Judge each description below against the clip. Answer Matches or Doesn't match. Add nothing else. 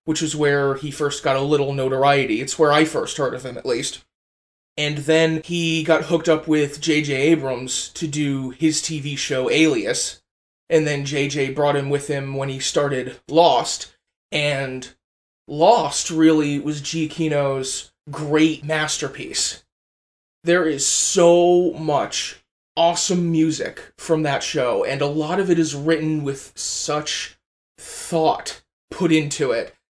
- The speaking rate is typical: Matches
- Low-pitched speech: Doesn't match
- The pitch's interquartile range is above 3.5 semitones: Doesn't match